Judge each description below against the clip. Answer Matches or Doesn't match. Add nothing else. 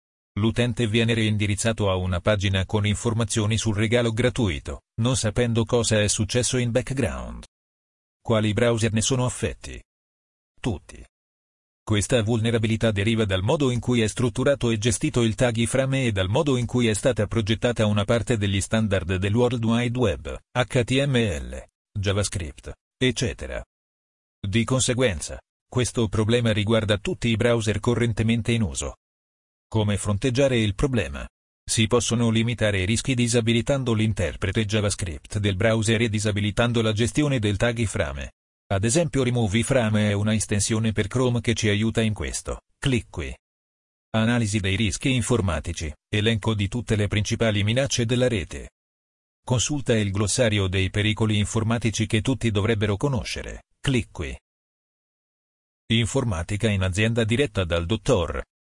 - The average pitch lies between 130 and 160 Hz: Doesn't match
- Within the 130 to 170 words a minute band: Matches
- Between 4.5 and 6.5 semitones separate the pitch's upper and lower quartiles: Doesn't match